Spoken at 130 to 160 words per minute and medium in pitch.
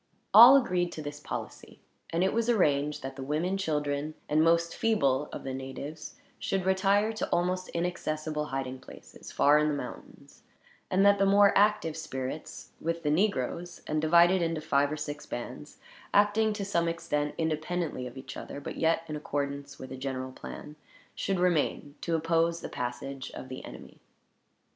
No: average, 170 wpm; medium, 155 Hz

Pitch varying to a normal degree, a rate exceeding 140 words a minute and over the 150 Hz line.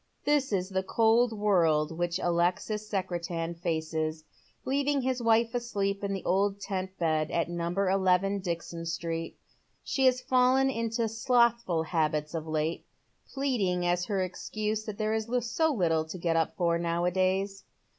Yes: average, 4.9 semitones; average, 155 wpm; high, 190 Hz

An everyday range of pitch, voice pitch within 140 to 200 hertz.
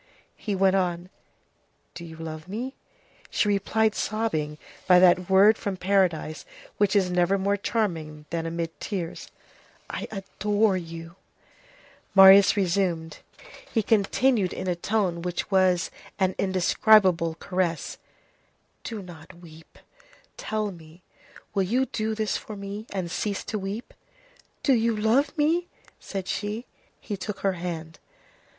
Yes: average, 3.5 semitones; high, 190 Hz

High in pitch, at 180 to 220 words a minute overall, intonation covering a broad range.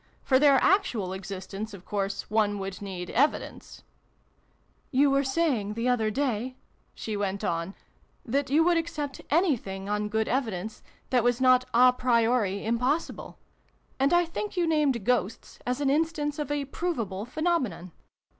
No: very high, 250 Hz; average, 160 wpm; wide, 5.9 semitones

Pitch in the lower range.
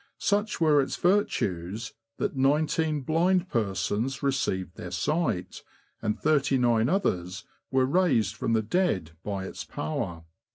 Yes: low, 125 Hz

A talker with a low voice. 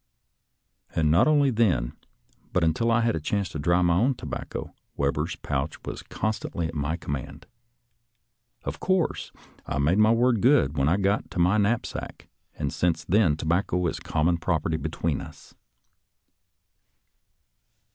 Yes: very low, 85 Hz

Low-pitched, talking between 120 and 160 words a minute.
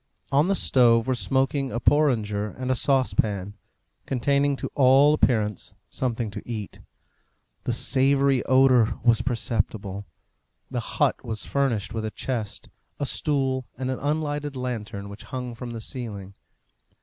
Yes: low, 125 Hz; average, 140 wpm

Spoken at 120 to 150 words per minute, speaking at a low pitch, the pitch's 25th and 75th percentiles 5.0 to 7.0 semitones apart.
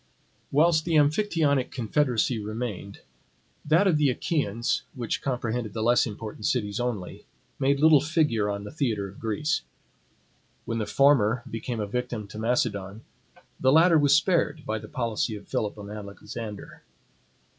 Yes: average, 145 wpm; low, 120 Hz; wide, 5.4 semitones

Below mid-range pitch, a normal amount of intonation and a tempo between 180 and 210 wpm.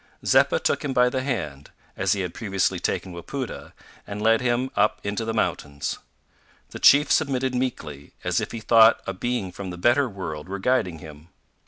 No: low, 105 Hz; wide, 5.7 semitones; average, 185 wpm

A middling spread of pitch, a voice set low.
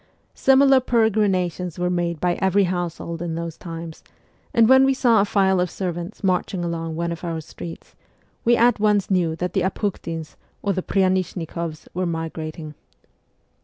No: average, 3.2 semitones; medium, 180 Hz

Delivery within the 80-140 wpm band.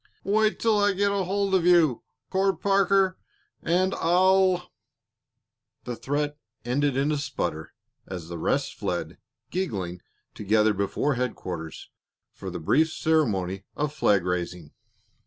Yes: slow, 135 wpm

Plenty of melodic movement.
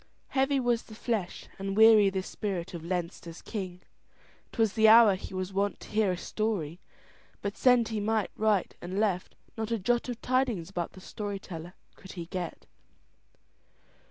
No: average, 3.4 semitones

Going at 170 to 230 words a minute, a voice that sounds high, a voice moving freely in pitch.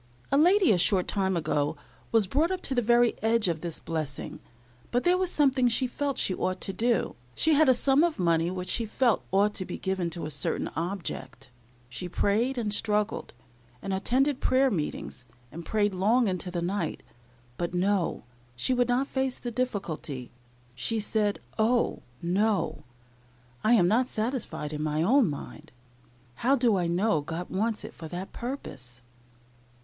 Yes: average, 175 wpm; high, 205 Hz; wide, 6.2 semitones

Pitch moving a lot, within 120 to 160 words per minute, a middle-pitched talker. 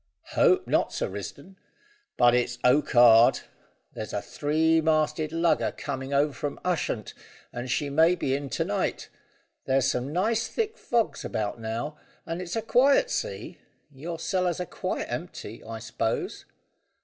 Yes: wide, 5.9 semitones; average, 150 wpm; medium, 145 Hz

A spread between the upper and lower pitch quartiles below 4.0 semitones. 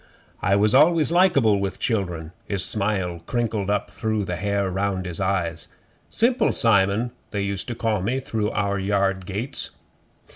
Yes: average, 2.8 semitones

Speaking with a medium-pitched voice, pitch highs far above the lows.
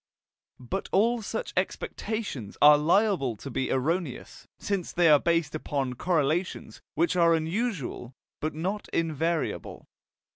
No: medium, 165 Hz; average, 4.9 semitones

